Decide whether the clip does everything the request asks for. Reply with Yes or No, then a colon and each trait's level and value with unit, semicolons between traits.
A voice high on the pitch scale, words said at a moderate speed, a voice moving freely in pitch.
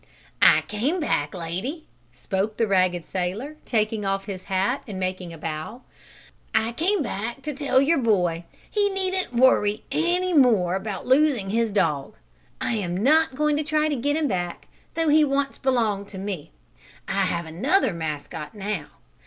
Yes: high, 215 Hz; average, 165 wpm; wide, 7.6 semitones